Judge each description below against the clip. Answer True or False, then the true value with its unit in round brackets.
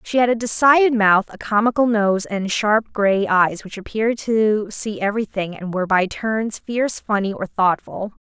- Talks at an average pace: True (180 wpm)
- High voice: True (210 Hz)